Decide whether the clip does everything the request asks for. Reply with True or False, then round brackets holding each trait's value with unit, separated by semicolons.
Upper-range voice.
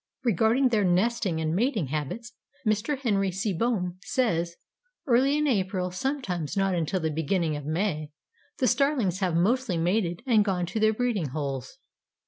True (195 Hz)